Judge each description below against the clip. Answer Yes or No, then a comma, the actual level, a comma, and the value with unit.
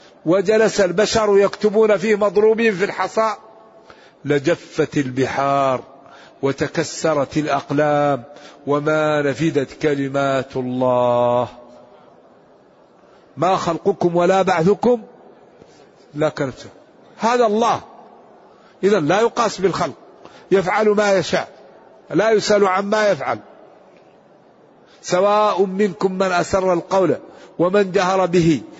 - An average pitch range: No, wide, 6.2 semitones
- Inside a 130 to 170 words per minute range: No, average, 90 wpm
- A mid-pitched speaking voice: Yes, medium, 180 Hz